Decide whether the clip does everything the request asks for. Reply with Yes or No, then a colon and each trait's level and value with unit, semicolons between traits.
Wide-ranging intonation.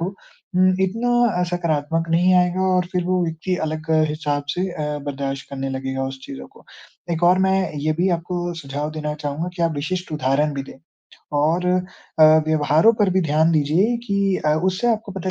No: average, 3.7 semitones